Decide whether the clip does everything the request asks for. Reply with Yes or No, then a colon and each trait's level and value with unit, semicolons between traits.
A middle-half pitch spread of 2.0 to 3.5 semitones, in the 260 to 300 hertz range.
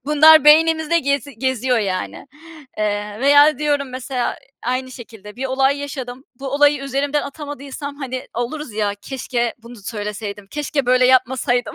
Yes: average, 3.1 semitones; very high, 265 Hz